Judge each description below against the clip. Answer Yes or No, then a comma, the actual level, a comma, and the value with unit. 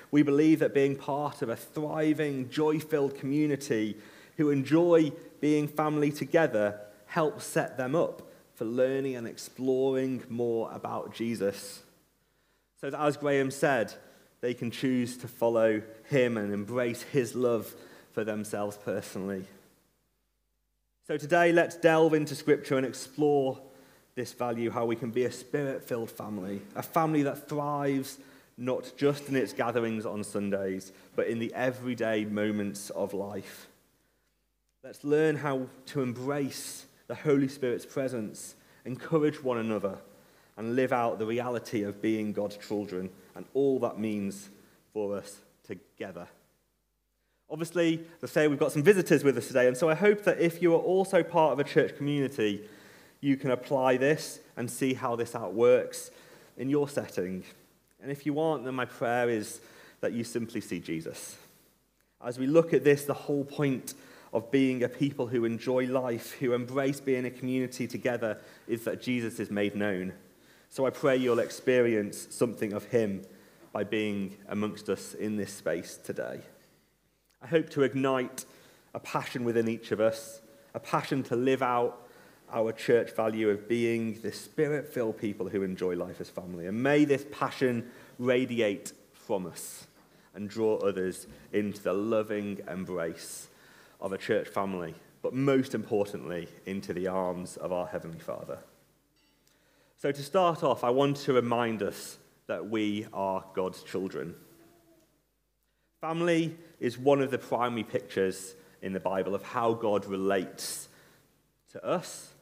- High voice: No, low, 125 Hz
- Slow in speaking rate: No, average, 155 wpm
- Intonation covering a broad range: No, average, 5.0 semitones